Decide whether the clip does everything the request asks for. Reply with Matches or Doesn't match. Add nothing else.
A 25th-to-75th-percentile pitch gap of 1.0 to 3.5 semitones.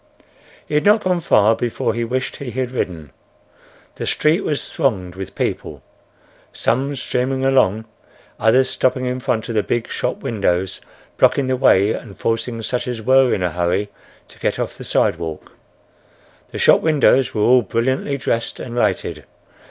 Doesn't match